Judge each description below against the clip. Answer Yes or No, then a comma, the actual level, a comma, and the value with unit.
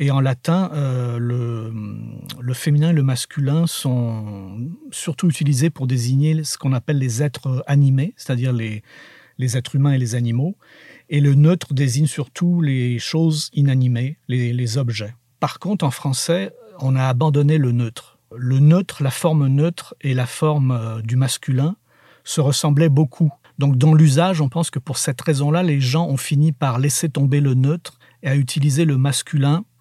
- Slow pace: No, average, 175 wpm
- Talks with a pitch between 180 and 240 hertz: No, medium, 140 Hz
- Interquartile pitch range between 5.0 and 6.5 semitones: No, average, 3.4 semitones